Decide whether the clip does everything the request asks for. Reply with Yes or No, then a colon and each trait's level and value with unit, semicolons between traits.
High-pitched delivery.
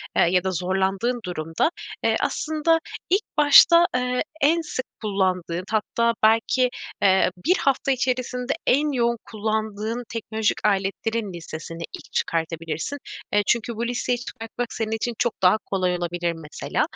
Yes: high, 220 Hz